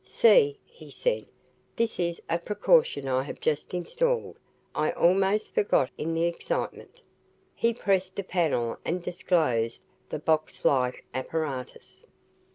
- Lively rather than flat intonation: Yes, wide, 6.0 semitones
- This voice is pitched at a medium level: Yes, medium, 170 Hz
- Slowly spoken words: Yes, slow, 130 wpm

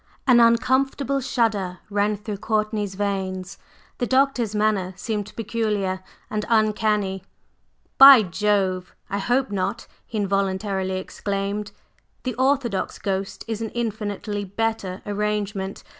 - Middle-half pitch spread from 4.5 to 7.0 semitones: No, narrow, 2.6 semitones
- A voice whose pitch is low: No, high, 210 Hz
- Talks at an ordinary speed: No, slow, 115 wpm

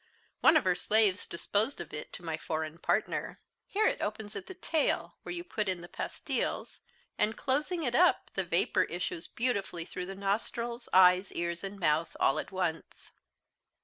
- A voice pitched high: Yes, high, 200 Hz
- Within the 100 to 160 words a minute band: No, average, 180 wpm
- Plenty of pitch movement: Yes, wide, 5.8 semitones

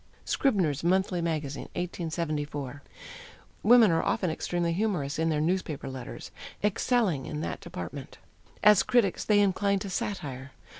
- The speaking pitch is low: No, medium, 170 Hz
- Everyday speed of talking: No, slow, 130 wpm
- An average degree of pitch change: Yes, average, 5.0 semitones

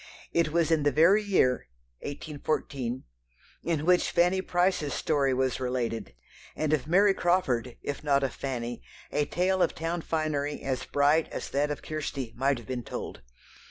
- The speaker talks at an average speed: Yes, average, 160 wpm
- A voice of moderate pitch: Yes, medium, 145 Hz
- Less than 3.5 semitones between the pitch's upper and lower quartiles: No, average, 4.2 semitones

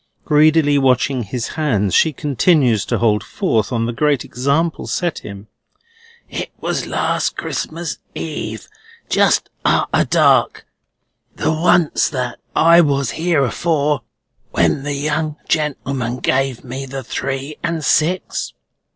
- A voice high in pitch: No, medium, 140 Hz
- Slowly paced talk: Yes, slow, 125 wpm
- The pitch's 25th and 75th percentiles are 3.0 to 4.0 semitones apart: Yes, average, 3.7 semitones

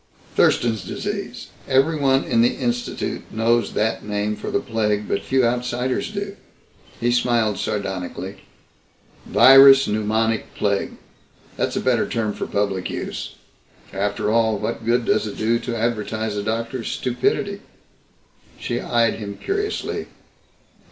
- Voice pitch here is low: Yes, low, 115 Hz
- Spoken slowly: Yes, slow, 130 wpm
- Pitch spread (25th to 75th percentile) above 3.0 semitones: No, average, 2.7 semitones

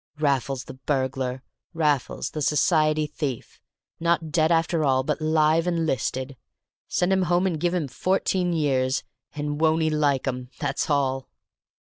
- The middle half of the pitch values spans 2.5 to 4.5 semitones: Yes, average, 3.4 semitones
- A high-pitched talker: No, medium, 150 Hz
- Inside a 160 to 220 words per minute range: No, average, 150 wpm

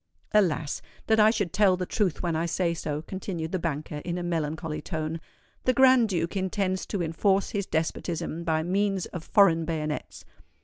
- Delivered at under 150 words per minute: No, average, 175 wpm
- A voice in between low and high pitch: Yes, medium, 175 Hz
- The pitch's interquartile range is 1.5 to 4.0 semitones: Yes, average, 3.5 semitones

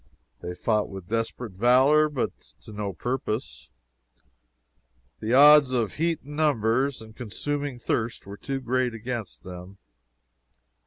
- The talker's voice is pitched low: Yes, low, 120 Hz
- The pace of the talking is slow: Yes, slow, 125 wpm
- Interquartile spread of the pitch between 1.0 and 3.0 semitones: No, average, 4.3 semitones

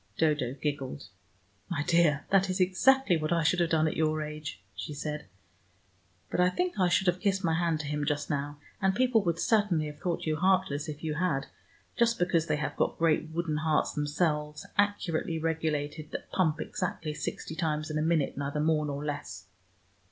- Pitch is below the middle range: No, medium, 160 Hz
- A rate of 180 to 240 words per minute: Yes, average, 190 wpm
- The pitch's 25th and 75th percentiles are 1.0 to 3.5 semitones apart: Yes, average, 2.9 semitones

